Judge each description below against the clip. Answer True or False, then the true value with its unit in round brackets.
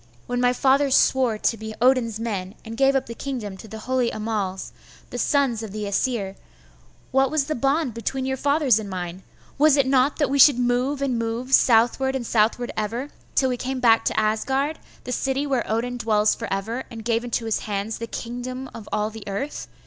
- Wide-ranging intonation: False (3.4 semitones)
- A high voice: True (240 Hz)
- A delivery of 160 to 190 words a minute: False (205 wpm)